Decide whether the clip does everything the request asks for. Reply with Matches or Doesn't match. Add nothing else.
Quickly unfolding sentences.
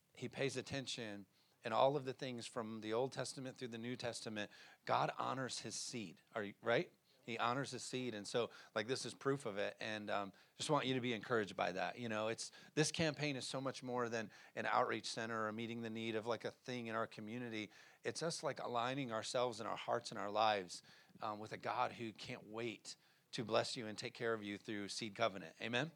Matches